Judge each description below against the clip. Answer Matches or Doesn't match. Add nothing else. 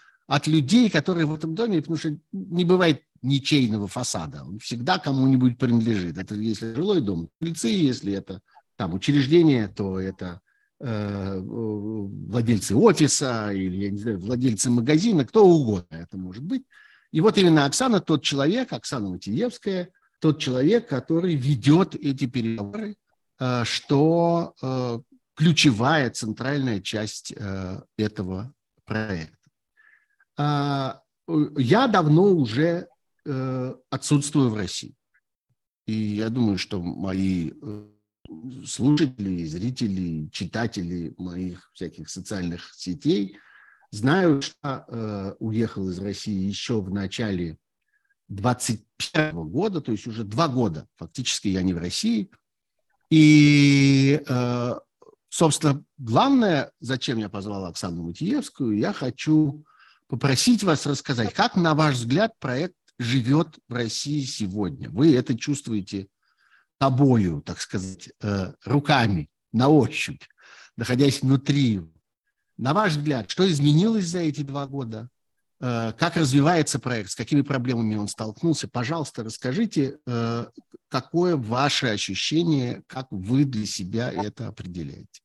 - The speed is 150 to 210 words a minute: Doesn't match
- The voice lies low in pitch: Matches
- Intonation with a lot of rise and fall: Matches